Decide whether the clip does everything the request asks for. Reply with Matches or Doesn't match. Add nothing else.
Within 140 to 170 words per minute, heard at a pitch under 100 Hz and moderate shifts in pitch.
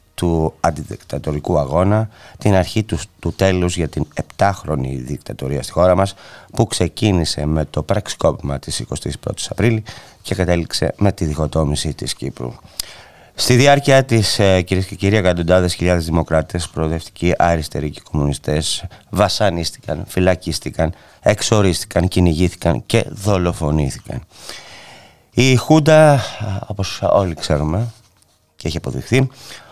Doesn't match